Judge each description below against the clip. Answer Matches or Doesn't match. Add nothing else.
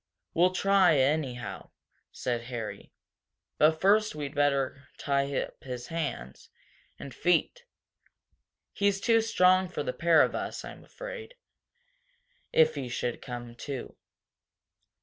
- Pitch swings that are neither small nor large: Doesn't match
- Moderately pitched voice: Matches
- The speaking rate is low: Matches